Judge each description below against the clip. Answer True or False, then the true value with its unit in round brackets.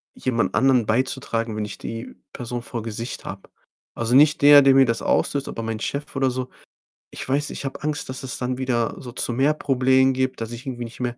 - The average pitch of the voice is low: True (125 Hz)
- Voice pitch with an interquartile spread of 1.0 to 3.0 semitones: True (2.5 semitones)